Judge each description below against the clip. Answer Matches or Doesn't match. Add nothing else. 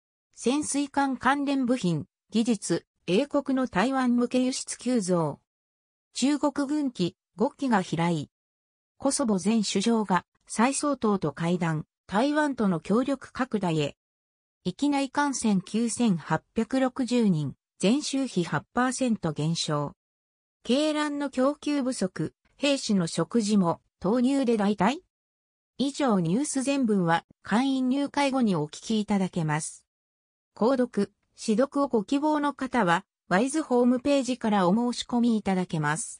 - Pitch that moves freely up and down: Matches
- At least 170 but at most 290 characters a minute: Matches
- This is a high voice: Matches